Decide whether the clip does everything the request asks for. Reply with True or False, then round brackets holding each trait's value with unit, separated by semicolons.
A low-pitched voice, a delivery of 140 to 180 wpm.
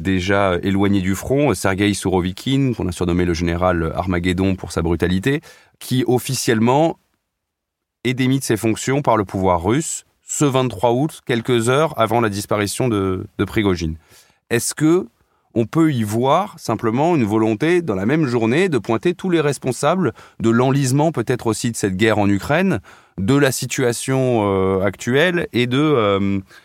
True (115 Hz; 160 wpm)